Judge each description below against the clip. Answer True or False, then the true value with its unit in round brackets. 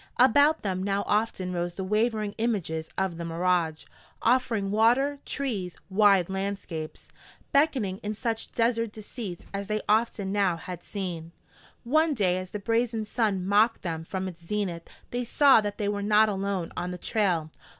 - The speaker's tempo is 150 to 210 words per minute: True (160 wpm)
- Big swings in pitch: False (3.8 semitones)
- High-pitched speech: True (200 Hz)